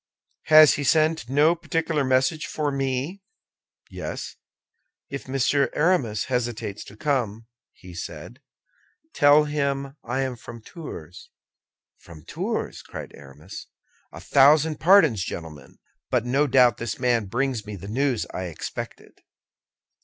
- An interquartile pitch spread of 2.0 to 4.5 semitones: No, average, 5.2 semitones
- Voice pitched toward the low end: Yes, low, 130 Hz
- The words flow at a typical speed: No, slow, 125 wpm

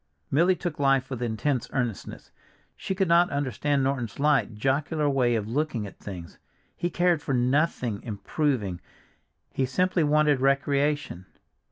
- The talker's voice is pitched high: No, medium, 140 Hz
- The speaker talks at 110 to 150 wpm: Yes, average, 140 wpm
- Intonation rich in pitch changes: No, average, 3.9 semitones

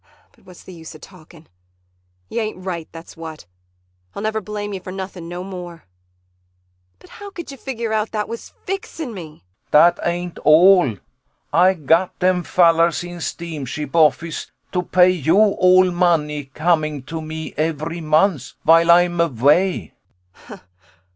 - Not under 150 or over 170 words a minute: Yes, average, 155 wpm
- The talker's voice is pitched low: No, medium, 175 Hz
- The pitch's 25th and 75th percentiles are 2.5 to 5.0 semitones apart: Yes, average, 2.8 semitones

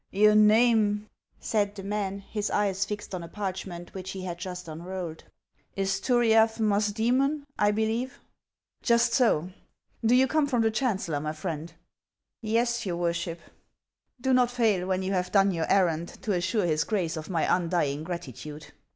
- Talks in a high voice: Yes, high, 195 Hz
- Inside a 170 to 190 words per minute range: Yes, average, 185 wpm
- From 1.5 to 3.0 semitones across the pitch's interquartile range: No, average, 4.1 semitones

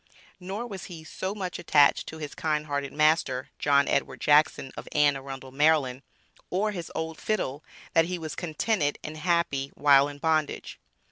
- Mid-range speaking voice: Yes, medium, 155 Hz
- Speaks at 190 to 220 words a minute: No, average, 165 wpm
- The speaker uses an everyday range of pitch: Yes, average, 3.2 semitones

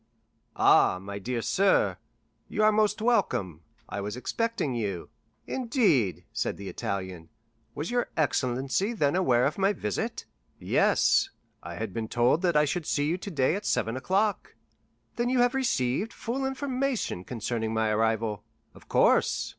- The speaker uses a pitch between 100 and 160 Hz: Yes, medium, 140 Hz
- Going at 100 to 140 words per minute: No, average, 150 wpm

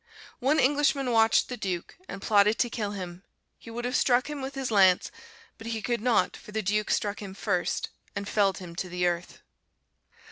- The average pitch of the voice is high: Yes, high, 210 Hz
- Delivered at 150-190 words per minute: No, average, 200 wpm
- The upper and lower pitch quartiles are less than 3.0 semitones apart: No, average, 4.2 semitones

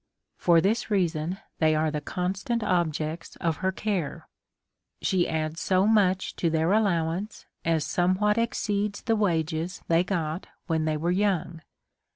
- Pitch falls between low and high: Yes, medium, 175 Hz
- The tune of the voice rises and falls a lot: No, average, 3.8 semitones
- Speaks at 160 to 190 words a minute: No, average, 150 wpm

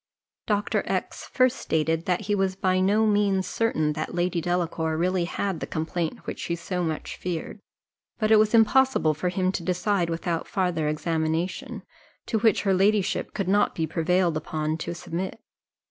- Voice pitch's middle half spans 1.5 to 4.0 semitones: Yes, average, 3.6 semitones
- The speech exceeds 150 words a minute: Yes, average, 170 wpm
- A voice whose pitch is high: No, medium, 180 Hz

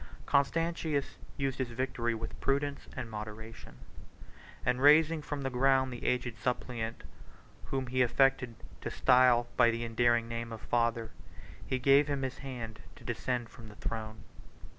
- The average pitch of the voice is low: Yes, low, 125 Hz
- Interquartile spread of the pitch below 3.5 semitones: Yes, average, 2.7 semitones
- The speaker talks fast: No, average, 150 wpm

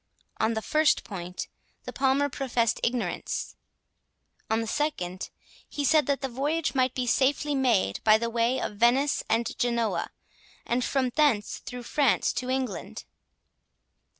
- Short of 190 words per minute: Yes, average, 145 wpm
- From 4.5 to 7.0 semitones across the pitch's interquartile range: No, average, 3.4 semitones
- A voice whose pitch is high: Yes, very high, 250 Hz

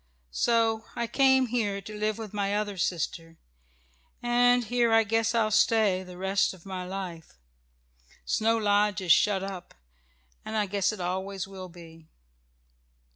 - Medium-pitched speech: No, high, 205 Hz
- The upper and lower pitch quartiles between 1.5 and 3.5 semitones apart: Yes, average, 3.2 semitones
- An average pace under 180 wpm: Yes, average, 150 wpm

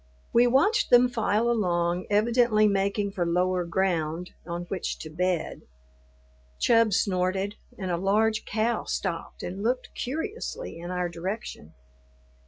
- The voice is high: Yes, high, 195 Hz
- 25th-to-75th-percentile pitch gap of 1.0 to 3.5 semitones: No, average, 4.2 semitones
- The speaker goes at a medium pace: No, slow, 130 wpm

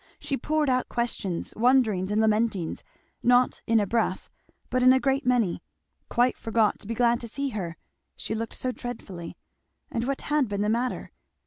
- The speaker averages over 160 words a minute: Yes, average, 180 wpm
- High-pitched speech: Yes, high, 235 Hz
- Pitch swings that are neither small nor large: Yes, average, 3.1 semitones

